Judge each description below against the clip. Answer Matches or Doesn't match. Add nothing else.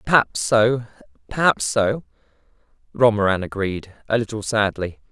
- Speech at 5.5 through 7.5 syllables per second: Doesn't match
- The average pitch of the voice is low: Matches